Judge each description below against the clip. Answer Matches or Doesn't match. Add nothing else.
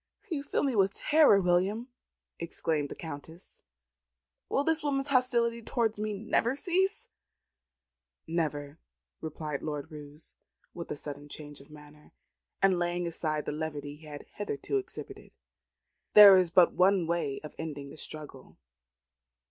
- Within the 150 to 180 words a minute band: Doesn't match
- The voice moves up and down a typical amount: Doesn't match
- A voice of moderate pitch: Matches